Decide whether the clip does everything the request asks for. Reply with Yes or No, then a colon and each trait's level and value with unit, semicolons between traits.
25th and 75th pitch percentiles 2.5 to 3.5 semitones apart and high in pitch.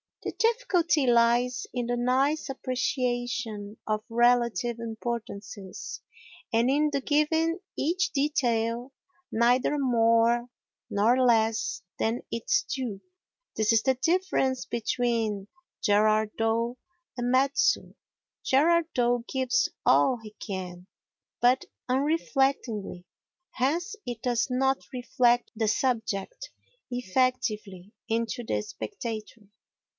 Yes: average, 3.0 semitones; high, 245 Hz